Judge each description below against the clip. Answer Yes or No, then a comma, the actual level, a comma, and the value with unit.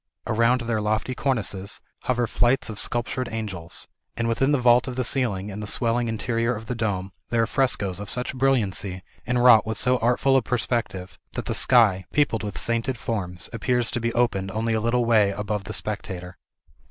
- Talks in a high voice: No, low, 115 Hz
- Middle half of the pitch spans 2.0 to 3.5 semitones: Yes, average, 3.0 semitones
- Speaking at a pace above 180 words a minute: Yes, average, 190 wpm